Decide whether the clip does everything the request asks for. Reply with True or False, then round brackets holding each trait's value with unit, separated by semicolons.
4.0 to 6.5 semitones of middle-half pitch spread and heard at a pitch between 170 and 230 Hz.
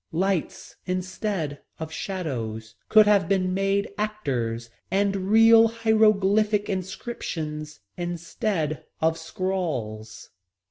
True (5.0 semitones; 185 Hz)